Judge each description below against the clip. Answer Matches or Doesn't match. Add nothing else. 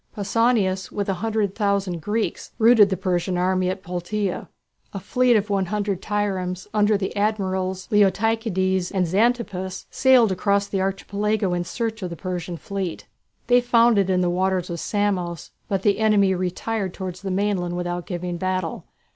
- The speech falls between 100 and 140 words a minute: Doesn't match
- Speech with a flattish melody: Matches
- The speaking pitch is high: Matches